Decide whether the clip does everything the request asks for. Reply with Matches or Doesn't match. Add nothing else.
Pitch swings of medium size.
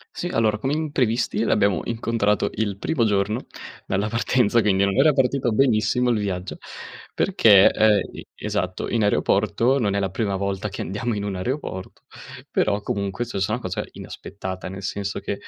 Matches